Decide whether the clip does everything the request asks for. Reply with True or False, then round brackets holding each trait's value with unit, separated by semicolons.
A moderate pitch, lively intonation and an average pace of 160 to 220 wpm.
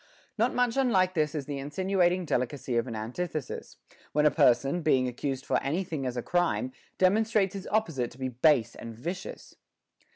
True (155 Hz; 6.4 semitones; 185 wpm)